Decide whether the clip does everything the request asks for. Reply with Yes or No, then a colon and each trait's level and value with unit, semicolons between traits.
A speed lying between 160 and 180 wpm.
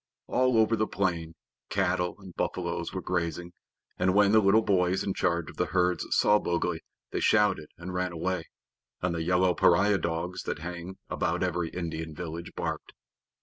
Yes: average, 170 wpm